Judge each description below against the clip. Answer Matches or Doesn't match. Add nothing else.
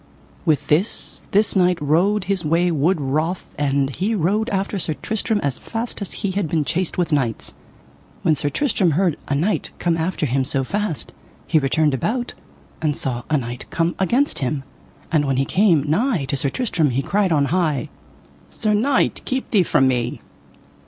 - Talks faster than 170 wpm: Matches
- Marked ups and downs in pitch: Matches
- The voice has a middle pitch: Matches